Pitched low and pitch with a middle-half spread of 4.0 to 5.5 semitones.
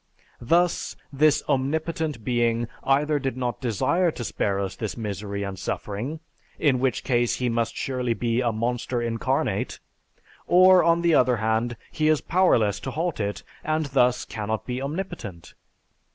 Yes: low, 125 Hz; average, 5.1 semitones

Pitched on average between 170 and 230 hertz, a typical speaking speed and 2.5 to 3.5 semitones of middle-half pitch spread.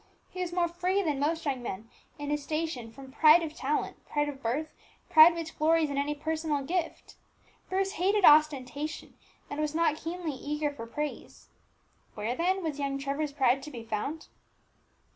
No: very high, 300 Hz; average, 175 wpm; average, 2.9 semitones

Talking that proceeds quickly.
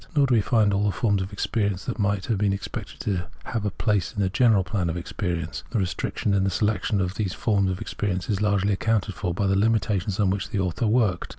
Yes: fast, 240 wpm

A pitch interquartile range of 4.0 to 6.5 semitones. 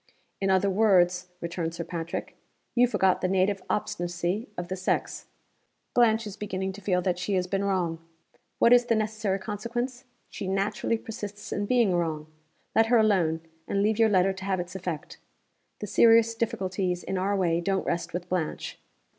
No: average, 3.1 semitones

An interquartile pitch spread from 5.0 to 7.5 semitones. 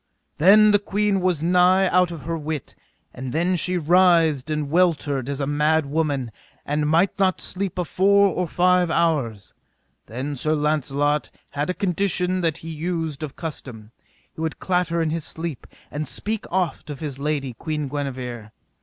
No: average, 3.7 semitones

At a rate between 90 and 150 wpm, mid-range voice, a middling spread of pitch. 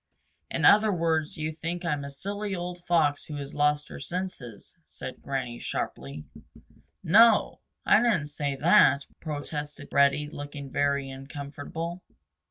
Yes: average, 140 wpm; medium, 150 Hz; average, 3.5 semitones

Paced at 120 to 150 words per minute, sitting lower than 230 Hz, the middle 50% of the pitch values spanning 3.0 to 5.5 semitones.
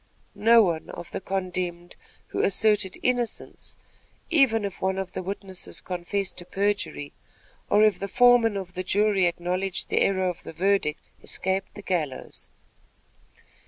No: average, 140 wpm; high, 190 Hz; narrow, 2.4 semitones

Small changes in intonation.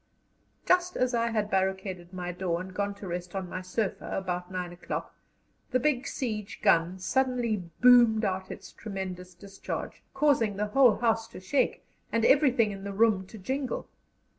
No: average, 4.3 semitones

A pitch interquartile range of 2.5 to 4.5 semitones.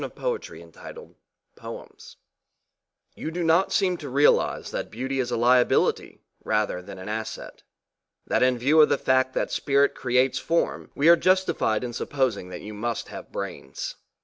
No: wide, 5.6 semitones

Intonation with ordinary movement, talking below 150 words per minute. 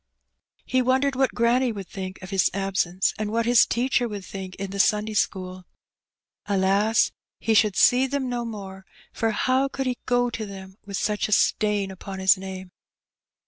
No: average, 4.1 semitones; average, 180 wpm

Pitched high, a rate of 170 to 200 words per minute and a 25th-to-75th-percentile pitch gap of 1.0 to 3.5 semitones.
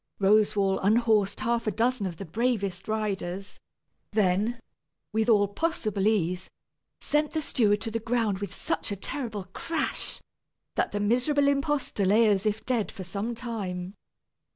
No: high, 215 Hz; average, 150 wpm; average, 3.1 semitones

